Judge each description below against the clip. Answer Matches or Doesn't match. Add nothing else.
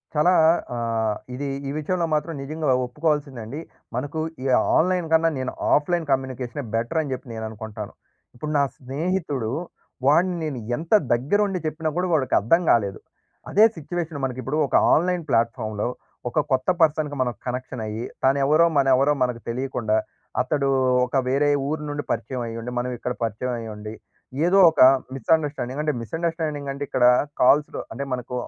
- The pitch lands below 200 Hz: Matches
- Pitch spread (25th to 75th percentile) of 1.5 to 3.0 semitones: Doesn't match